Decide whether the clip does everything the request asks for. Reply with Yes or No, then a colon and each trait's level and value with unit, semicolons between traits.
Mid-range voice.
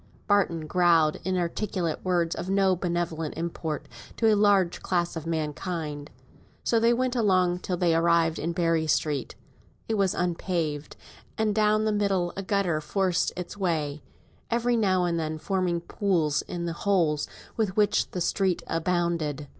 Yes: medium, 175 Hz